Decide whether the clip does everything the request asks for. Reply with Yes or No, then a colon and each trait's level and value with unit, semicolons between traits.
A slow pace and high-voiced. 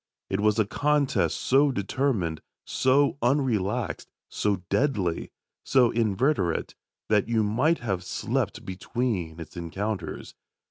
No: slow, 110 wpm; low, 110 Hz